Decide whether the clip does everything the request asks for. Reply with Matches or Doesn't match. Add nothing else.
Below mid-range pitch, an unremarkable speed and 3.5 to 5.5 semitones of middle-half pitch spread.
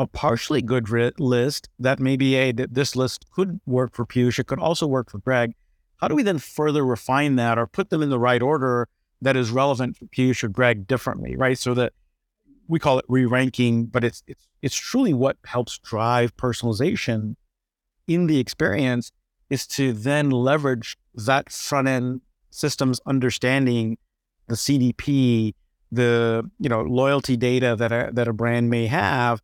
Doesn't match